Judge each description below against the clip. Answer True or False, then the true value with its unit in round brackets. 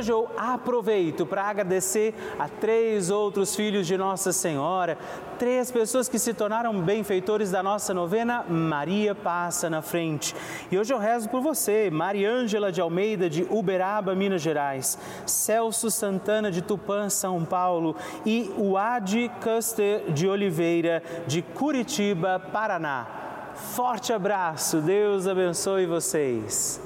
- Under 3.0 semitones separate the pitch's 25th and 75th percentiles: False (3.4 semitones)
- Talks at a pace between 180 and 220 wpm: False (125 wpm)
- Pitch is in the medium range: False (200 Hz)